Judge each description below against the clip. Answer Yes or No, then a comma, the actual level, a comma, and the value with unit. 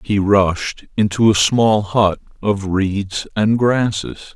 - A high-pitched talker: No, low, 105 Hz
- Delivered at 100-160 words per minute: Yes, average, 140 wpm